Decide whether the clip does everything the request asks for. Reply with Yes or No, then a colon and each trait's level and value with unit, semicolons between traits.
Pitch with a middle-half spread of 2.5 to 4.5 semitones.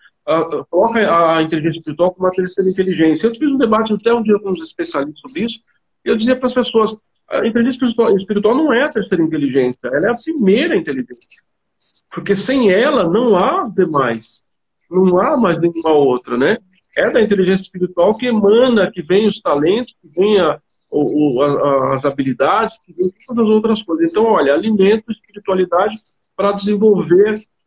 No: average, 4.9 semitones